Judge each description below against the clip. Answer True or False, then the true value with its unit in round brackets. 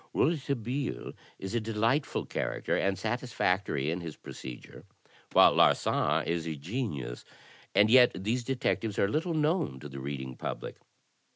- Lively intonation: True (8.6 semitones)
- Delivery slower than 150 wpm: True (135 wpm)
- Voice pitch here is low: True (105 Hz)